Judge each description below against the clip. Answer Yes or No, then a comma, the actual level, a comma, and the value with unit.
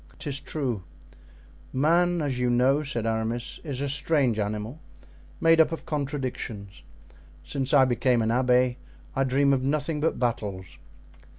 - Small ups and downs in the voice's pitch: No, average, 3.6 semitones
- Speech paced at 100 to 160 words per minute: Yes, average, 140 wpm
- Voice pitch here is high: No, low, 130 Hz